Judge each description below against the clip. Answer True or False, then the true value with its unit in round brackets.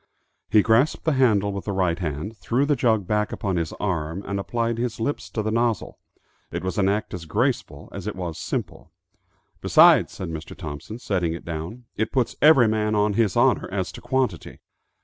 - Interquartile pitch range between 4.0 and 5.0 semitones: True (4.4 semitones)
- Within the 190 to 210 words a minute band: True (195 wpm)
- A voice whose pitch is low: True (105 Hz)